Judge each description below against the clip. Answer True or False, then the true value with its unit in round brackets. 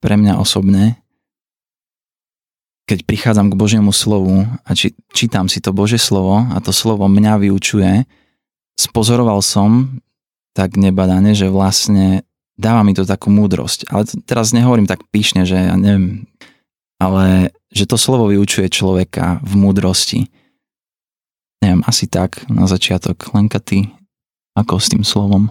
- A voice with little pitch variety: True (2.2 semitones)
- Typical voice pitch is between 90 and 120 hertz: True (100 Hz)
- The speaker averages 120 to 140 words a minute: True (135 wpm)